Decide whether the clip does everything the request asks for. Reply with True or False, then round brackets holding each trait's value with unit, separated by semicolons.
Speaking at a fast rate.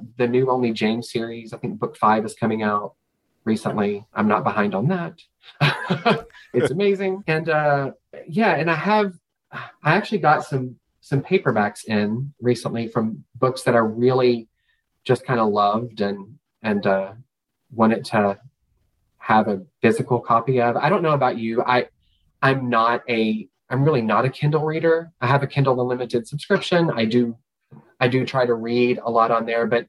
False (175 wpm)